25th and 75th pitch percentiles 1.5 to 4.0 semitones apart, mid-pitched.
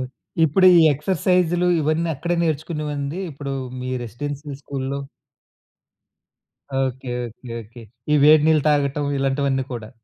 Yes: average, 2.8 semitones; medium, 145 Hz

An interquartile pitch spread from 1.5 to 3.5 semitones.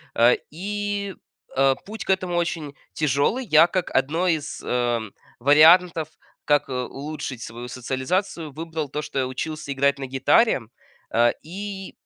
No: average, 5.2 semitones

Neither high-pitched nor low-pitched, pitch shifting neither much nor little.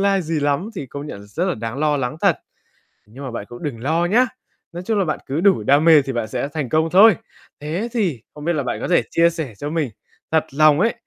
Yes: medium, 155 Hz; average, 4.2 semitones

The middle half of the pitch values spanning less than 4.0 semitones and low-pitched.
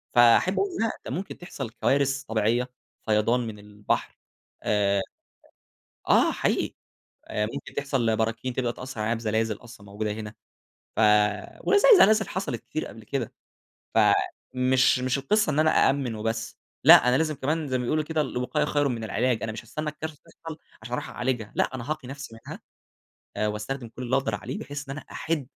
No: average, 4.3 semitones; low, 125 Hz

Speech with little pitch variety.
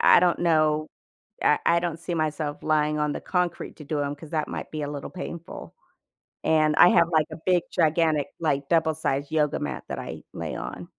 Yes: narrow, 2.0 semitones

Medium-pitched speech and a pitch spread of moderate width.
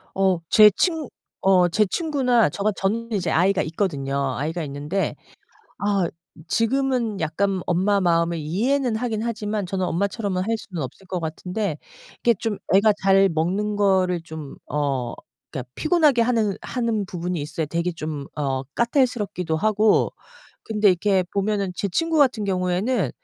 No: high, 195 Hz; average, 4.6 semitones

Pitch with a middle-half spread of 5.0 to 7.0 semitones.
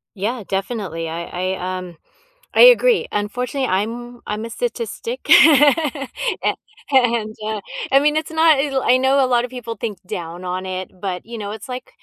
Yes: wide, 5.6 semitones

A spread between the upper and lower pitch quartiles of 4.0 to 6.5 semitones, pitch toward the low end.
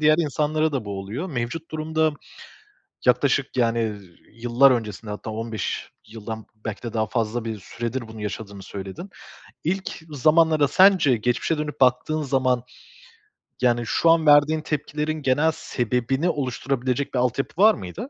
Yes: average, 5.3 semitones; low, 130 Hz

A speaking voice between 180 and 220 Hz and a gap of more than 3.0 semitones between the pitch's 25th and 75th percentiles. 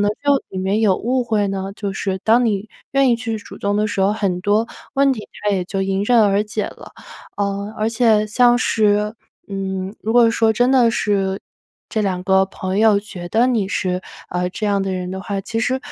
No: high, 205 Hz; average, 2.7 semitones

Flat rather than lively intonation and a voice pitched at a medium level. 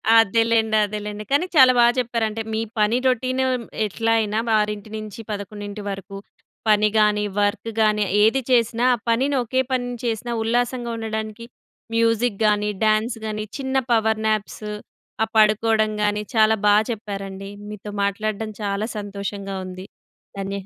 No: narrow, 1.8 semitones; high, 215 Hz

